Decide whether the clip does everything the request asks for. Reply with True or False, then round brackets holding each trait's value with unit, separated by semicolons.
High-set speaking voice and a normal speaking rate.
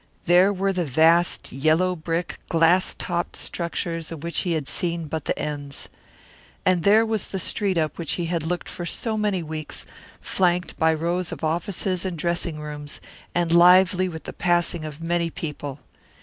False (170 Hz; 175 wpm)